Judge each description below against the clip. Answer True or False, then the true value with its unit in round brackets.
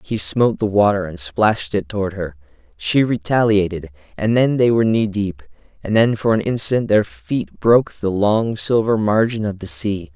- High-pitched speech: False (100 Hz)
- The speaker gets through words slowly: False (190 wpm)